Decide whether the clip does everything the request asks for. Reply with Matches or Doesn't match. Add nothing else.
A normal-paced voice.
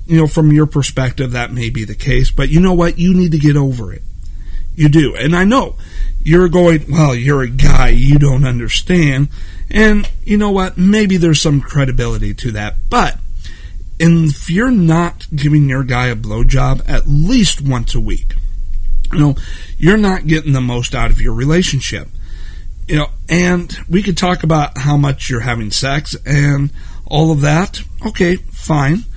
Matches